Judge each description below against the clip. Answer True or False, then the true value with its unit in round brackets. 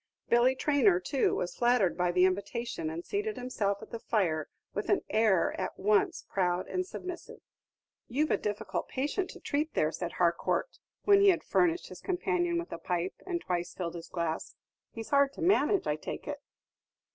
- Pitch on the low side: False (230 Hz)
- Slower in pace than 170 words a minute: False (180 wpm)